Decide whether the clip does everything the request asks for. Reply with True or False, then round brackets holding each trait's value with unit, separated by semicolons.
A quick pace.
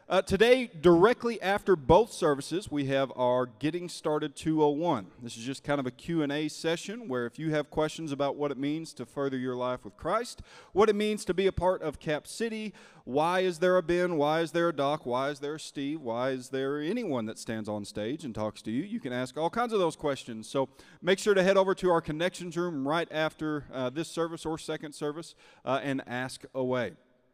True (225 wpm)